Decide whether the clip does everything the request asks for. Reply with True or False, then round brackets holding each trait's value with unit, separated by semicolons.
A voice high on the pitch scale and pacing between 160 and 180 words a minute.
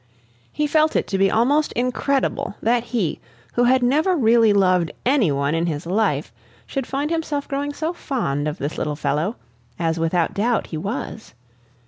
True (225 Hz; 170 wpm)